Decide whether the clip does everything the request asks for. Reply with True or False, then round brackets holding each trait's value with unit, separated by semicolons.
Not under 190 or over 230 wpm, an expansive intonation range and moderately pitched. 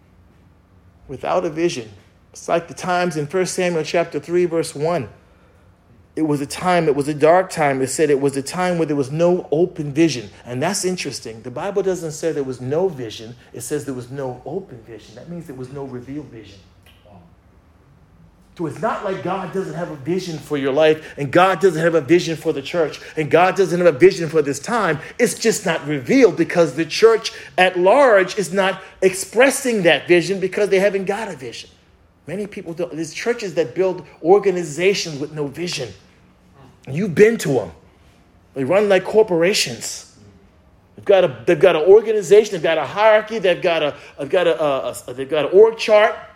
True (200 wpm; 6.8 semitones; 165 Hz)